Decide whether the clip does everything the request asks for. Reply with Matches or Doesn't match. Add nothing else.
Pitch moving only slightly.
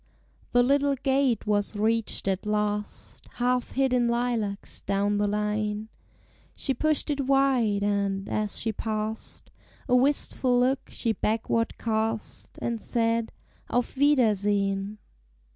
Doesn't match